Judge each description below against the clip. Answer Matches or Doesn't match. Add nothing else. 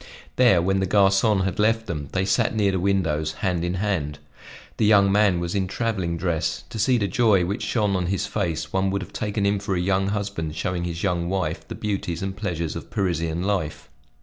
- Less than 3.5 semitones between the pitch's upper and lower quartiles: Matches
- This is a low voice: Matches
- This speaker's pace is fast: Matches